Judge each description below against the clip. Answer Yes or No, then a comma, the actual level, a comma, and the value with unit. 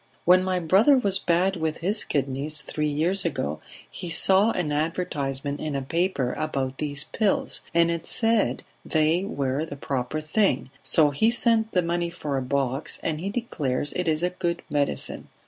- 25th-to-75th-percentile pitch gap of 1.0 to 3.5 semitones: No, average, 4.4 semitones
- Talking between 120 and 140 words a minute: No, average, 175 wpm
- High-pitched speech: No, medium, 160 Hz